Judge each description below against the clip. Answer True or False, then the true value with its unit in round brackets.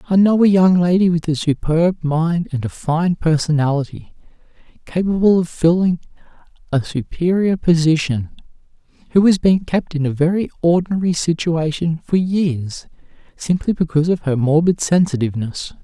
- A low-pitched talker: False (165 Hz)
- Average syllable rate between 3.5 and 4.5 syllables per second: False (4.9 syllables/s)